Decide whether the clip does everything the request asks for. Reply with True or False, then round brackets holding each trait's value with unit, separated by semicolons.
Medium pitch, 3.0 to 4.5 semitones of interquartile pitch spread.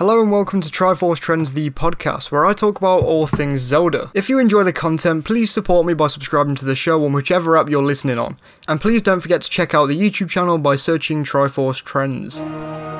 True (160 Hz; 4.1 semitones)